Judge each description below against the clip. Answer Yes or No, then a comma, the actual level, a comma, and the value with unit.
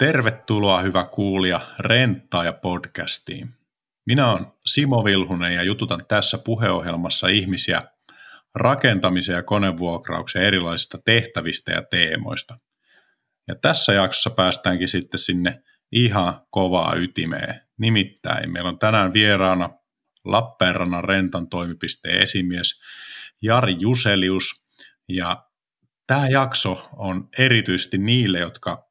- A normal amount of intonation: Yes, average, 3.9 semitones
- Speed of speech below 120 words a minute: Yes, average, 100 wpm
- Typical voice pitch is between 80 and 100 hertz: Yes, very low, 95 Hz